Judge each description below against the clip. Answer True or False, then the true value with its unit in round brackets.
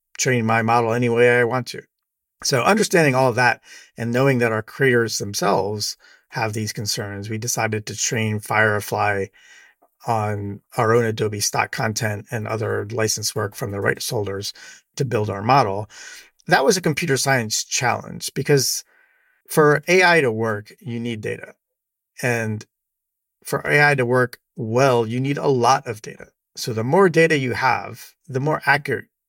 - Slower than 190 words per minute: True (165 wpm)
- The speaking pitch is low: True (120 Hz)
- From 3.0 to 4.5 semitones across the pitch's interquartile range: True (3.8 semitones)